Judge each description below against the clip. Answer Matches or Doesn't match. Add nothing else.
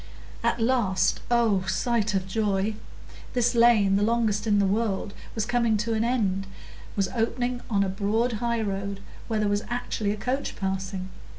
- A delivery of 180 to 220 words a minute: Doesn't match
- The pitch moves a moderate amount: Matches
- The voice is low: Doesn't match